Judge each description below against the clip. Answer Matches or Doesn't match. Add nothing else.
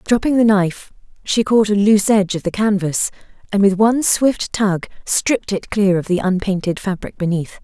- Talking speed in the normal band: Matches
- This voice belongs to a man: Doesn't match